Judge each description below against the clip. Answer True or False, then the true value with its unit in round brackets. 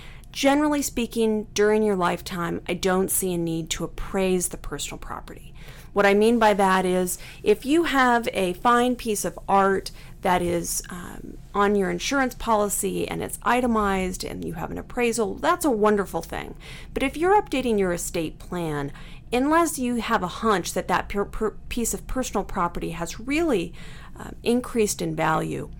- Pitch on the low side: False (200 Hz)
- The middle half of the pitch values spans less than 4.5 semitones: False (5.3 semitones)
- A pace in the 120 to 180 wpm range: True (170 wpm)